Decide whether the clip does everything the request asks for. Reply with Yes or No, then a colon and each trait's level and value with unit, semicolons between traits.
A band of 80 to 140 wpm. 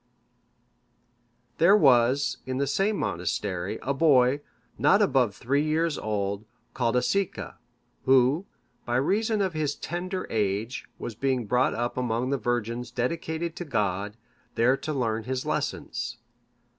Yes: slow, 135 wpm